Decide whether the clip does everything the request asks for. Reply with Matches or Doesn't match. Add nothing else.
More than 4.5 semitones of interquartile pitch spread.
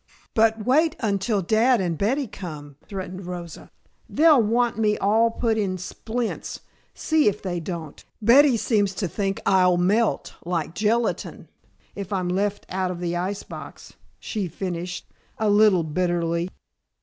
Doesn't match